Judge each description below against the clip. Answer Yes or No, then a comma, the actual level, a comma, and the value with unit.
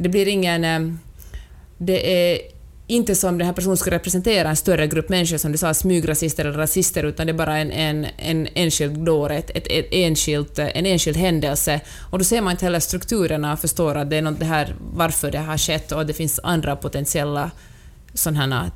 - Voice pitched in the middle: Yes, medium, 160 Hz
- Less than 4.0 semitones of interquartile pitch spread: Yes, average, 3.0 semitones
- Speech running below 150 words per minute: No, average, 190 wpm